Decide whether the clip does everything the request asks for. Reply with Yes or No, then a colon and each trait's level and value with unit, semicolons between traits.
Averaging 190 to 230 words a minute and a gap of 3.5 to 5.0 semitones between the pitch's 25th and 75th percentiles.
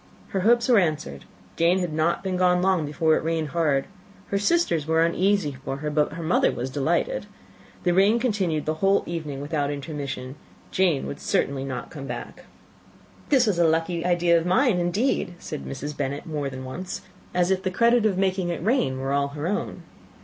Yes: average, 195 wpm; average, 4.4 semitones